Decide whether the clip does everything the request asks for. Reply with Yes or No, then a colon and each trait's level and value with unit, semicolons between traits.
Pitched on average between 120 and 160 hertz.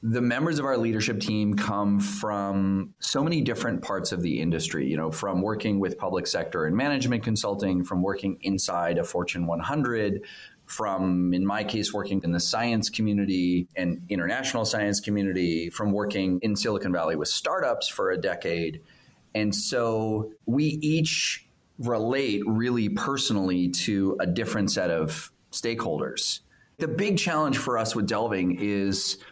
No: low, 105 Hz